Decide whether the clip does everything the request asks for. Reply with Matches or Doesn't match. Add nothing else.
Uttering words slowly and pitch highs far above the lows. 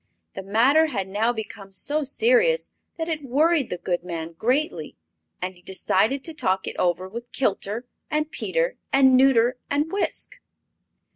Doesn't match